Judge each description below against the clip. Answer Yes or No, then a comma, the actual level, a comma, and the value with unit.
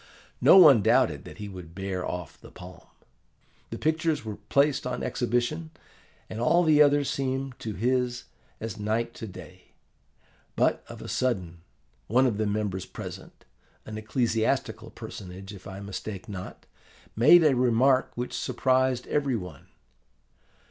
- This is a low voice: Yes, low, 115 Hz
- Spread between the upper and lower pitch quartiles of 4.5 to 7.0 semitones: Yes, average, 4.8 semitones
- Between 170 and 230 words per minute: No, average, 145 wpm